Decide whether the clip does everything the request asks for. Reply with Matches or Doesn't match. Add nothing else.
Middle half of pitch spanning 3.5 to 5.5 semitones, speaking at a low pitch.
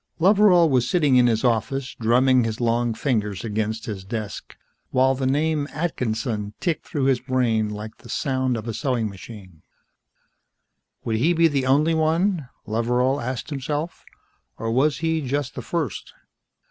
Matches